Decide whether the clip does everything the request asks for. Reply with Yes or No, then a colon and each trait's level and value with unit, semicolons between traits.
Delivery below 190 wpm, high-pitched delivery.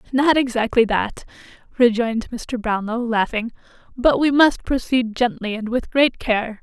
Yes: average, 145 wpm; high, 235 Hz